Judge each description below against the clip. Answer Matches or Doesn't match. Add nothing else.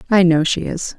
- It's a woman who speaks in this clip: Matches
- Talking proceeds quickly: Matches